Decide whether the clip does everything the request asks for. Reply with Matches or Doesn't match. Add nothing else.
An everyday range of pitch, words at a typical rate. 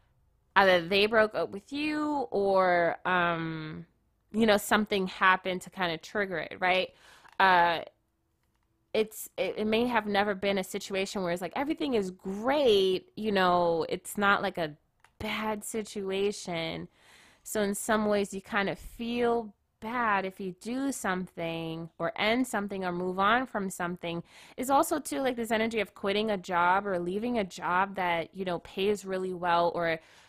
Matches